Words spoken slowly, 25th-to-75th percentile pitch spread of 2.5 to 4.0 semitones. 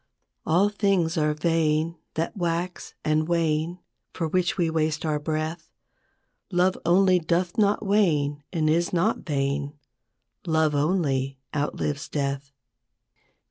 Yes: slow, 120 wpm; average, 2.8 semitones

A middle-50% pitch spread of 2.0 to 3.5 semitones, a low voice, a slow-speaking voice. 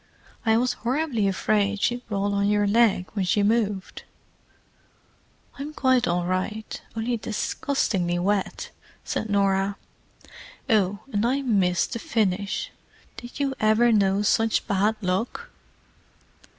No: average, 3.0 semitones; high, 210 Hz; slow, 115 wpm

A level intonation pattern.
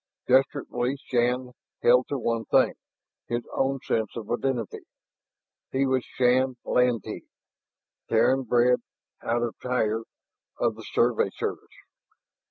Yes: narrow, 1.7 semitones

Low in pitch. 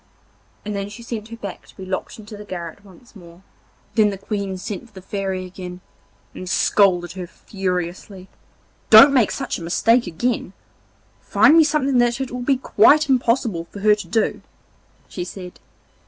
No: high, 205 Hz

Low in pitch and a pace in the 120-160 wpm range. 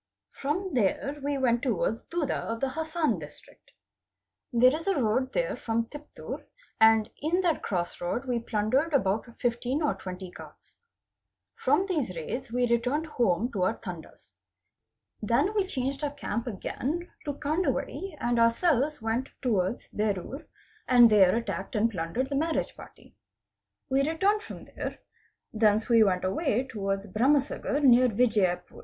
No: high, 245 Hz; average, 150 wpm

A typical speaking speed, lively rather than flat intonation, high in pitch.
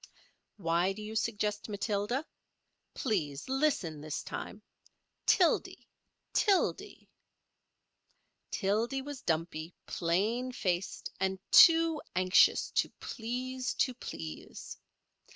No: slow, 80 wpm; wide, 6.5 semitones; high, 210 Hz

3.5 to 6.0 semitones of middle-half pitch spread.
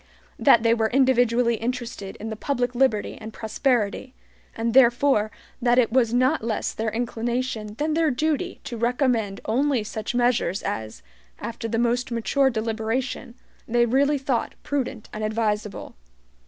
No: average, 2.8 semitones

